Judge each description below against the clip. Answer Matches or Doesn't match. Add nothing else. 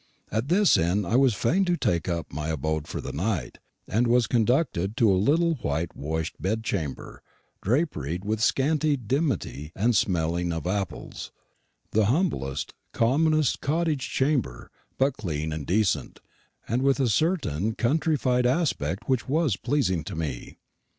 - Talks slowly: Doesn't match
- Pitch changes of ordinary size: Doesn't match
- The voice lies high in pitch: Doesn't match